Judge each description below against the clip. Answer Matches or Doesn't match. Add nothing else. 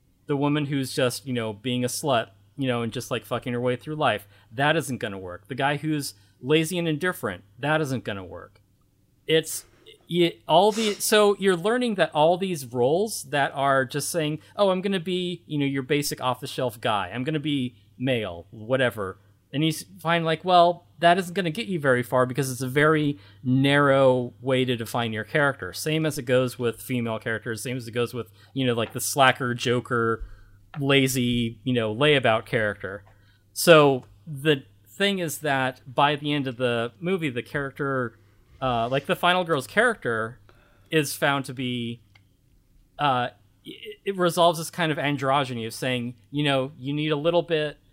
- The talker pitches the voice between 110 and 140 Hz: Matches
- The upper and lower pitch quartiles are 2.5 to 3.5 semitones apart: Doesn't match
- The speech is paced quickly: Doesn't match